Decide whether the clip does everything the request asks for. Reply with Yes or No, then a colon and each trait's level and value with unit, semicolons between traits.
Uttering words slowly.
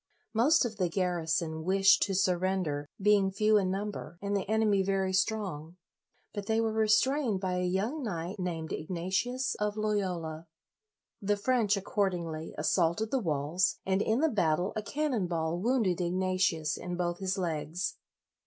No: average, 155 wpm